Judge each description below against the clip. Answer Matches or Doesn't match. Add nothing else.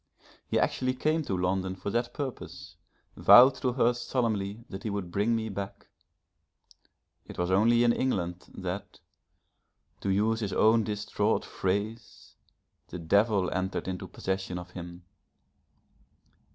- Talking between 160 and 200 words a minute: Doesn't match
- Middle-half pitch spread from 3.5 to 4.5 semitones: Matches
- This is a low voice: Matches